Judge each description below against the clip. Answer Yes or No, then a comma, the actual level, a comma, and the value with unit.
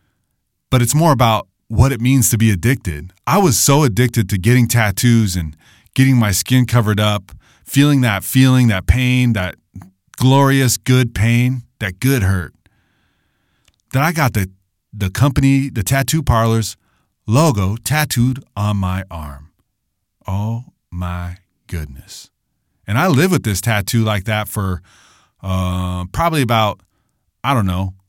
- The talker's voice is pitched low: Yes, low, 110 Hz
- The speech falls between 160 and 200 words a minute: No, average, 145 wpm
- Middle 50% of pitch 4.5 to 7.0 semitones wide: Yes, average, 5.1 semitones